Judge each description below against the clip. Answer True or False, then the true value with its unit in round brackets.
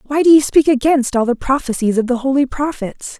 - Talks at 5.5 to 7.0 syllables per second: True (5.7 syllables/s)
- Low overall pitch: False (270 Hz)